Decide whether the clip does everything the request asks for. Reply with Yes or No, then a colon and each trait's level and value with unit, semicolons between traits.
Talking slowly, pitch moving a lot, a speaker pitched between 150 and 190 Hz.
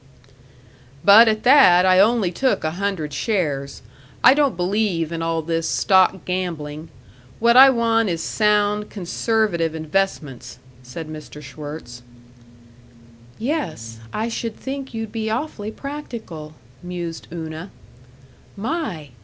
Yes: slow, 120 wpm; wide, 5.9 semitones; medium, 185 Hz